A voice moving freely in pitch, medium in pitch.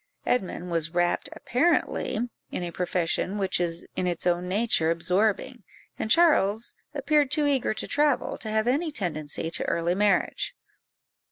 No: wide, 6.2 semitones; high, 195 Hz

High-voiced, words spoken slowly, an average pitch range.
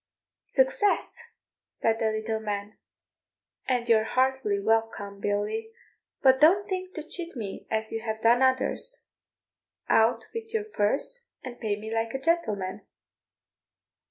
No: high, 230 Hz; slow, 130 wpm; wide, 7.4 semitones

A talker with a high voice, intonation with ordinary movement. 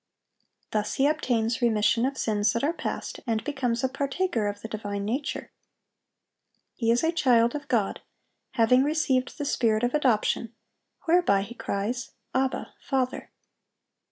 Yes: high, 245 Hz; average, 3.9 semitones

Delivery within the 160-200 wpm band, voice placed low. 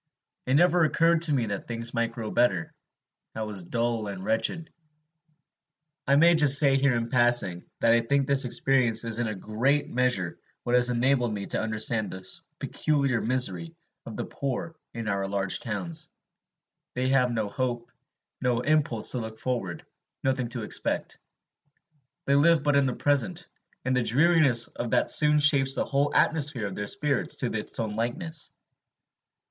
Yes: average, 170 wpm; low, 125 Hz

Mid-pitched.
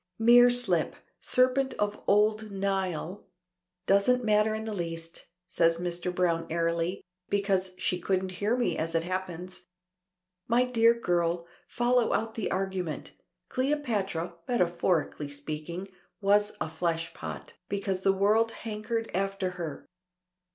No: high, 195 Hz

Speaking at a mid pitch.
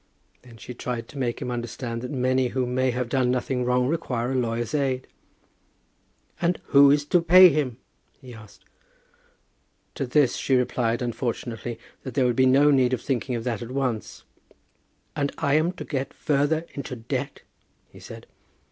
No: low, 130 Hz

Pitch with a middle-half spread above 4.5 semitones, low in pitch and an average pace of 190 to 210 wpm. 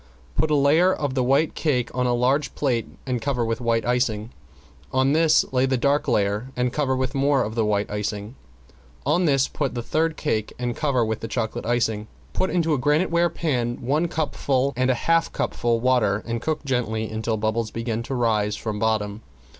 No: average, 4.0 semitones; low, 125 Hz; average, 195 wpm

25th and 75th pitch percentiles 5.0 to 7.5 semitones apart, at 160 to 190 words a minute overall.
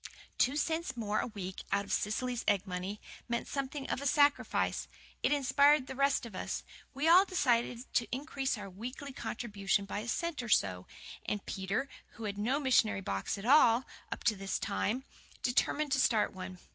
Yes: wide, 5.5 semitones; average, 185 wpm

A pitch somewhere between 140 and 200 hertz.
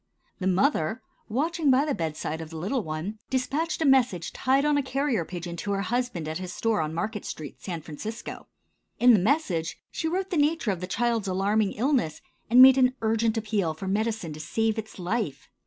No: high, 220 Hz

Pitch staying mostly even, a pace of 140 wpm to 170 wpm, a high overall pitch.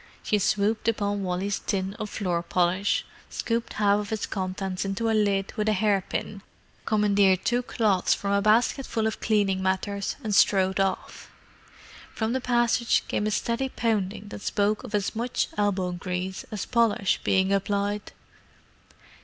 Yes: narrow, 2.1 semitones; average, 155 wpm; high, 205 Hz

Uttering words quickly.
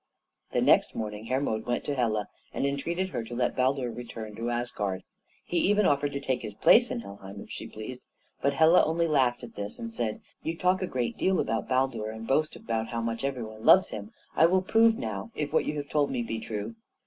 Yes: fast, 220 wpm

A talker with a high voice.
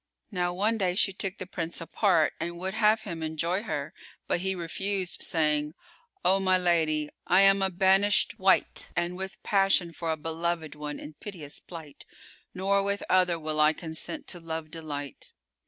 No: medium, 175 Hz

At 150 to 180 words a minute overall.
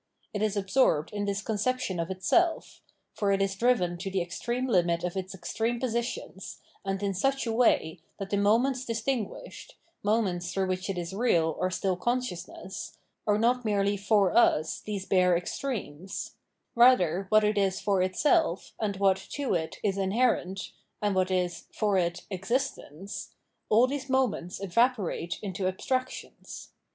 Yes: average, 160 wpm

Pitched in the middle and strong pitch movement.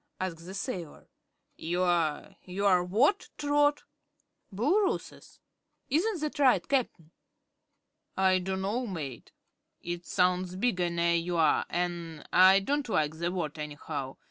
Yes: medium, 180 Hz; wide, 5.7 semitones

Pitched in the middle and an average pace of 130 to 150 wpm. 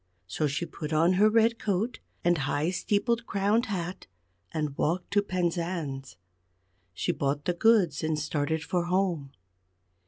Yes: medium, 175 Hz; average, 145 wpm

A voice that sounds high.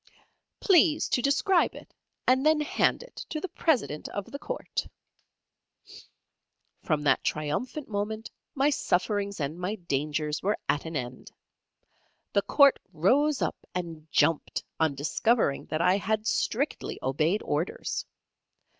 Yes: high, 200 Hz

